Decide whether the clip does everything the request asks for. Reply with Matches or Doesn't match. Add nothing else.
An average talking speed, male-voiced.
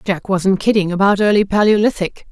Doesn't match